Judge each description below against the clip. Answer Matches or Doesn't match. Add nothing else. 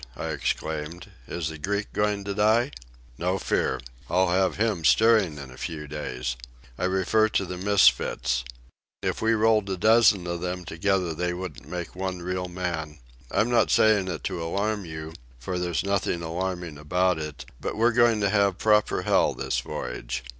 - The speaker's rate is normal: Matches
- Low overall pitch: Matches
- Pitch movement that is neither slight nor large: Matches